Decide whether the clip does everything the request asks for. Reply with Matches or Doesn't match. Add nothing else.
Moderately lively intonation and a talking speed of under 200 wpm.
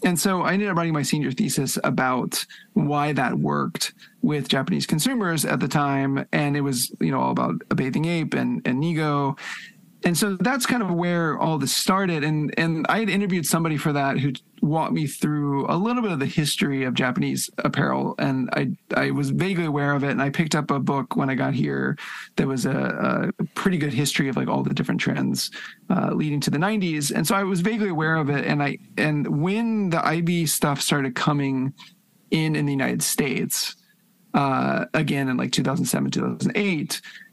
Doesn't match